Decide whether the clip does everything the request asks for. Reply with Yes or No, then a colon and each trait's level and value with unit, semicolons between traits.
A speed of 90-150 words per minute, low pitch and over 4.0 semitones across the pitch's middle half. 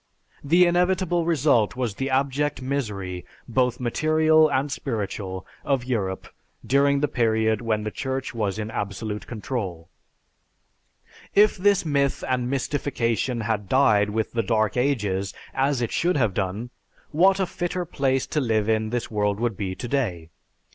Yes: average, 145 wpm; low, 125 Hz; average, 4.9 semitones